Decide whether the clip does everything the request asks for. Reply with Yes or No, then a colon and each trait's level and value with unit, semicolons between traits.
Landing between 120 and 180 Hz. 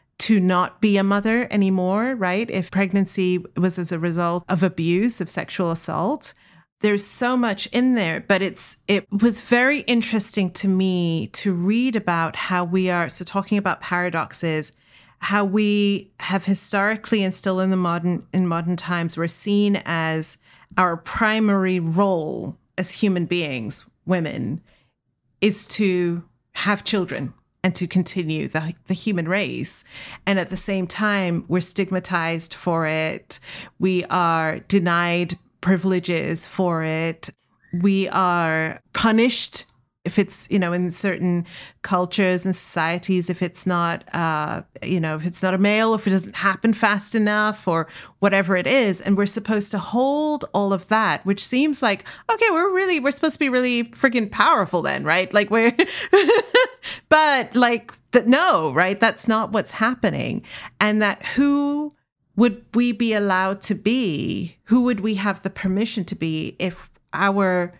No: high, 190 Hz